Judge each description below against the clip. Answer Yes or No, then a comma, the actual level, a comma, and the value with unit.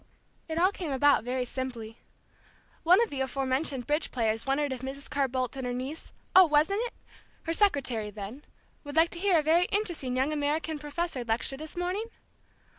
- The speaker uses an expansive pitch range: No, average, 4.2 semitones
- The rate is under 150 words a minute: No, average, 185 wpm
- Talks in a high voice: Yes, very high, 285 Hz